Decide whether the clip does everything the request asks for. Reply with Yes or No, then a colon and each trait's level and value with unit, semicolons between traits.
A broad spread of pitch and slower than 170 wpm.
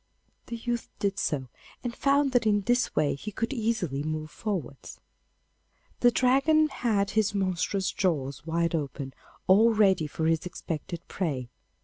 Yes: wide, 6.8 semitones; average, 145 wpm